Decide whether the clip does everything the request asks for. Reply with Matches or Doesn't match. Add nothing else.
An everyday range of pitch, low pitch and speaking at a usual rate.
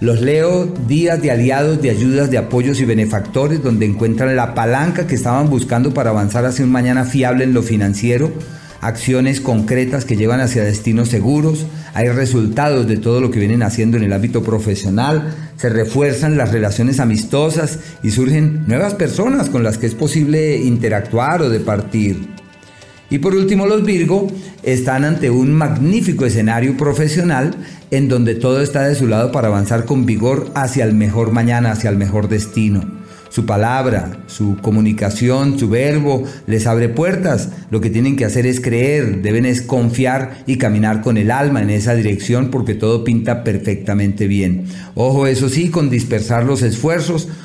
Matches